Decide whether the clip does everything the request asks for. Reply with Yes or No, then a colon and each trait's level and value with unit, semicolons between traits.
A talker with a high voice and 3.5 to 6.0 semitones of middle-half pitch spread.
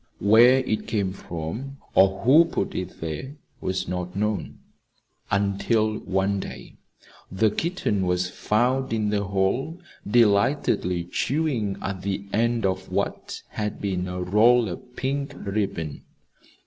No: low, 105 Hz; average, 4.4 semitones